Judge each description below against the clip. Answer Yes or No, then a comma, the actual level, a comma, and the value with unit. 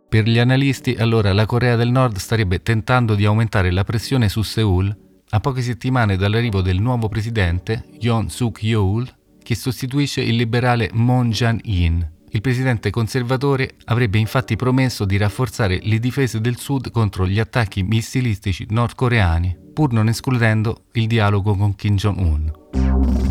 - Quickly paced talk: No, average, 150 wpm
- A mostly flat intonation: No, average, 3.5 semitones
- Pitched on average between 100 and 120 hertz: Yes, low, 115 Hz